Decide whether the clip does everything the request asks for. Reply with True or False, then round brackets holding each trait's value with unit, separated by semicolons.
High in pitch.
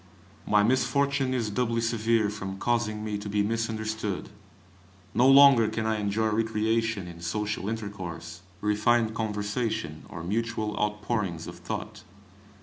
False (110 Hz)